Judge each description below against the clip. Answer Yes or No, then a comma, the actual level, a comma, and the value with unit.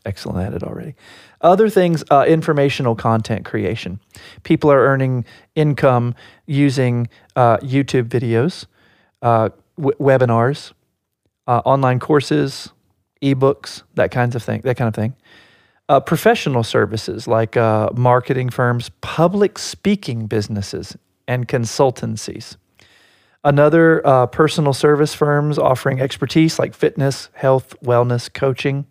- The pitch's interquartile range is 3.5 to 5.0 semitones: Yes, average, 4.1 semitones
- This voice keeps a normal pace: No, slow, 120 wpm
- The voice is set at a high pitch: No, low, 130 Hz